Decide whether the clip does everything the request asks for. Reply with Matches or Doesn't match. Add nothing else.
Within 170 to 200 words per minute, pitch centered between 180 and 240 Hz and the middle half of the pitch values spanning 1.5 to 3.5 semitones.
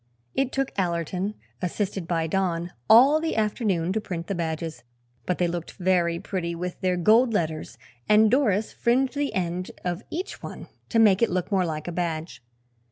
Doesn't match